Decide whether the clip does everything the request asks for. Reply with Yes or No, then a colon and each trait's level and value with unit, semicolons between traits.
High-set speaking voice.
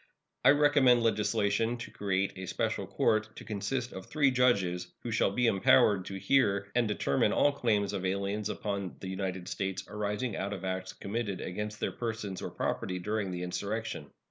No: low, 100 Hz